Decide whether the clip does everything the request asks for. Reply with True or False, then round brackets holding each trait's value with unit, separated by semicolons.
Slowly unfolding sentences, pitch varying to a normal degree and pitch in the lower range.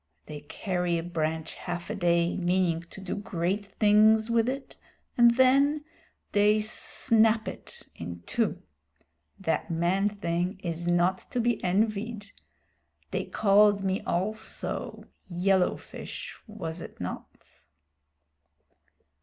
False (120 wpm; 3.9 semitones; 195 Hz)